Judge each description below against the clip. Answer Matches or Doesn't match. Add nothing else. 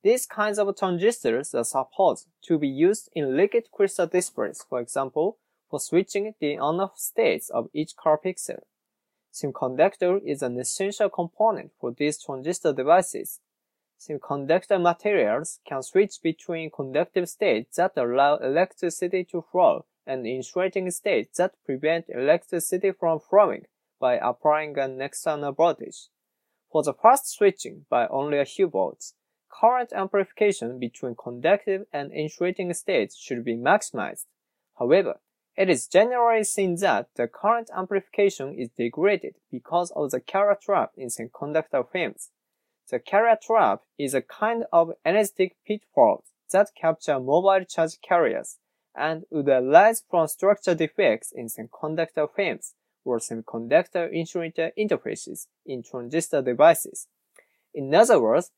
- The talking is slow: Matches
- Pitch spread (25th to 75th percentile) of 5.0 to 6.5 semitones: Matches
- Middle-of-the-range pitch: Matches